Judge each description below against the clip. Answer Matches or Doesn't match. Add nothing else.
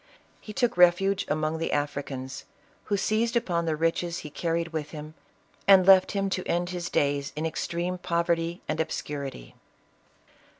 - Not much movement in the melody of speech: Doesn't match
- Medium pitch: Matches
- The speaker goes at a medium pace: Matches